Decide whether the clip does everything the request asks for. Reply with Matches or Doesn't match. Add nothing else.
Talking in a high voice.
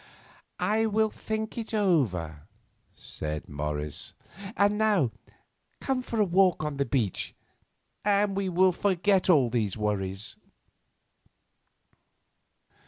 Doesn't match